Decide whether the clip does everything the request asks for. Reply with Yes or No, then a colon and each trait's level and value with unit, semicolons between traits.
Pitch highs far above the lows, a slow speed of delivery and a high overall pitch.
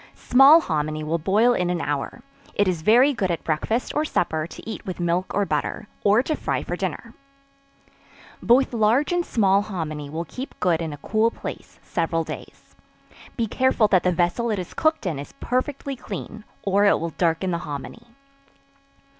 No: wide, 6.1 semitones; average, 180 wpm; high, 195 Hz